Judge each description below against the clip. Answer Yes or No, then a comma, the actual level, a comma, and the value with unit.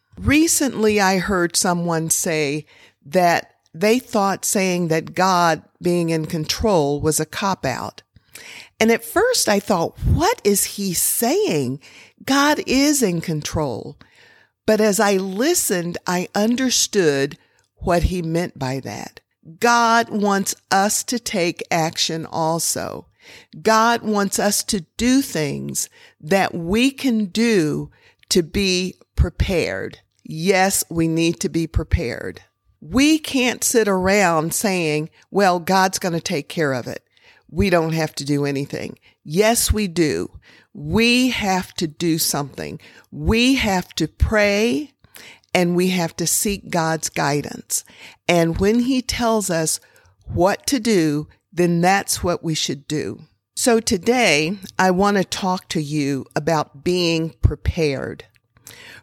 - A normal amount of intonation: Yes, average, 5.0 semitones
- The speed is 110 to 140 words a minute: Yes, slow, 135 wpm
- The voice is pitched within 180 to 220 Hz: Yes, medium, 185 Hz